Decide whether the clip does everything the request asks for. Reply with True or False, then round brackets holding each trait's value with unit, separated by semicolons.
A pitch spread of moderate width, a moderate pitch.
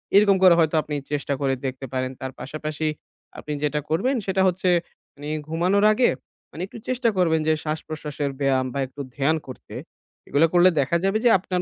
True (4.6 semitones; 155 Hz)